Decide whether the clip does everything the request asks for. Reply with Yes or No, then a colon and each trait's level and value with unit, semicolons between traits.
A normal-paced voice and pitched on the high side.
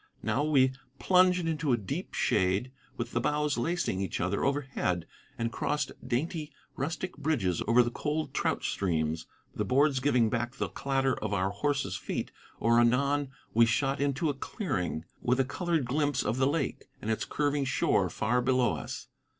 No: average, 170 wpm; low, 130 Hz